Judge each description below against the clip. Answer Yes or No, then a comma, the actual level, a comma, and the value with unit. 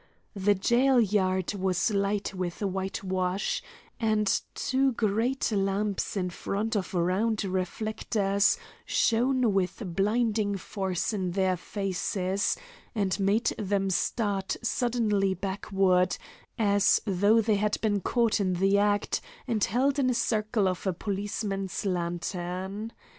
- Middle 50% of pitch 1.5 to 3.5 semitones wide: Yes, narrow, 2.5 semitones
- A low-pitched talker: No, high, 200 Hz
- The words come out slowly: Yes, slow, 120 wpm